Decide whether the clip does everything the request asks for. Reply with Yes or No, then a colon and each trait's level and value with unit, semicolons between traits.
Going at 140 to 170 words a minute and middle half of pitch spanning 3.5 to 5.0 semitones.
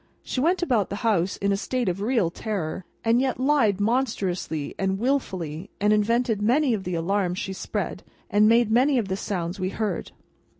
No: average, 185 wpm; average, 4.2 semitones